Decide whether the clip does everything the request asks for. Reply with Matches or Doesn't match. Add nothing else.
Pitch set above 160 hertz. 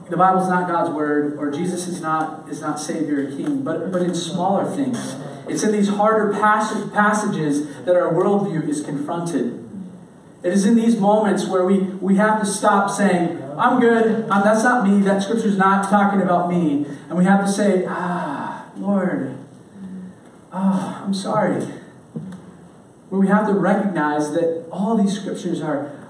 Matches